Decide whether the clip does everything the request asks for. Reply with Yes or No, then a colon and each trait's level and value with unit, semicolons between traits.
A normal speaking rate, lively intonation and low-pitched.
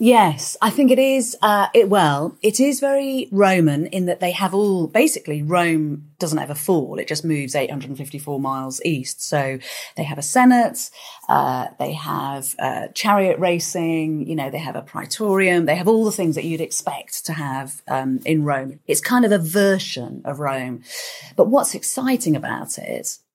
No: average, 180 wpm; wide, 5.7 semitones; medium, 165 Hz